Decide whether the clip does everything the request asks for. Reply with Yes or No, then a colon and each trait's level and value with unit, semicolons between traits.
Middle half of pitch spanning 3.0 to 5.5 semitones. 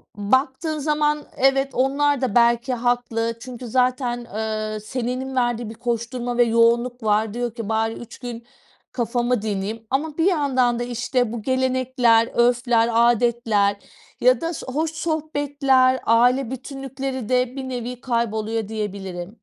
No: narrow, 2.4 semitones